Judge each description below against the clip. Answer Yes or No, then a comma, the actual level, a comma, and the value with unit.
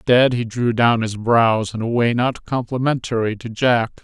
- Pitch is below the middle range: Yes, low, 120 Hz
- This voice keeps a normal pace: Yes, average, 195 wpm